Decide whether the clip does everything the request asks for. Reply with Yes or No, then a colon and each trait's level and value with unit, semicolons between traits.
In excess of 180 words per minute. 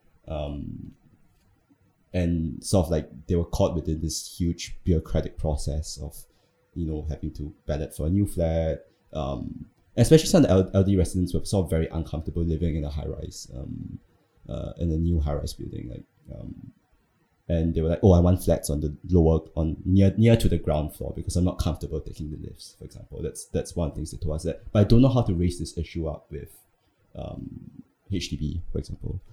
Yes: fast, 205 wpm